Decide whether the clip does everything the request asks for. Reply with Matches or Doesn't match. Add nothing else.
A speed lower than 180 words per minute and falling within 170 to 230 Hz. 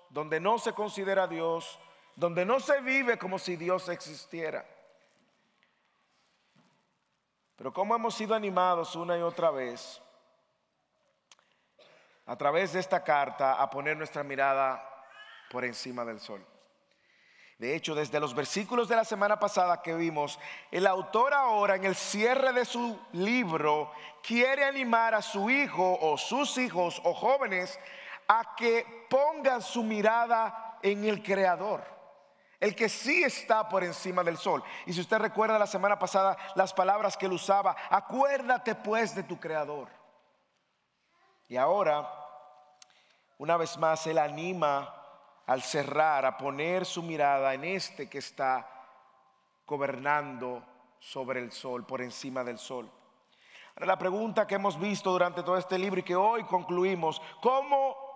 Matches